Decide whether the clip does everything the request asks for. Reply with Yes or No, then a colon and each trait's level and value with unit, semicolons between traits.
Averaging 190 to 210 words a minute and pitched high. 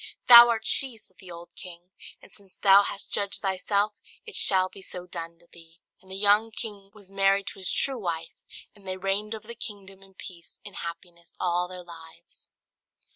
Yes: average, 195 wpm; high, 195 Hz